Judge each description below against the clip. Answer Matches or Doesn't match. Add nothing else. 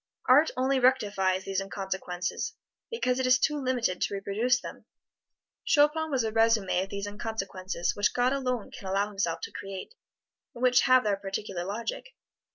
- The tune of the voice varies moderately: Matches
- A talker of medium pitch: Doesn't match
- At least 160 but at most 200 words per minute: Matches